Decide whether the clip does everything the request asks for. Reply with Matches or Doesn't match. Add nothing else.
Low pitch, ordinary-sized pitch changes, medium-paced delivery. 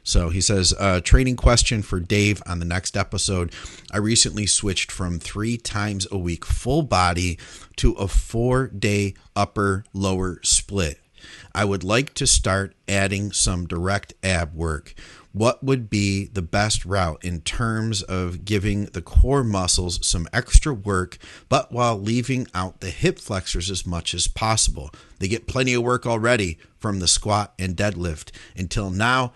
Matches